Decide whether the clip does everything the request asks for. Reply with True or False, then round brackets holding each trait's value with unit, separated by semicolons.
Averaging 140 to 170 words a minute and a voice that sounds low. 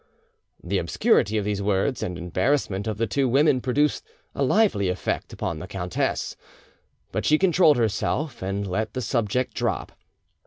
True (155 wpm; 110 Hz)